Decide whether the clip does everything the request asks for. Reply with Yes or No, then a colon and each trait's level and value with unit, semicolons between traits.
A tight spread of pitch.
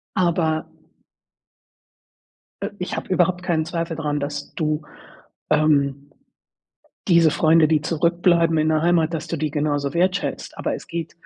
Yes: narrow, 2.0 semitones